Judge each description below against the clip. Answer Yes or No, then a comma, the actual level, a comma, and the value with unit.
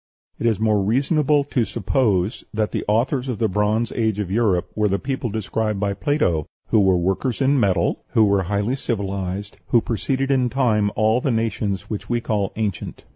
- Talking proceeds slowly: No, average, 185 wpm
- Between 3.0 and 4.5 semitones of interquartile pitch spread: Yes, average, 3.6 semitones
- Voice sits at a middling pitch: No, low, 110 Hz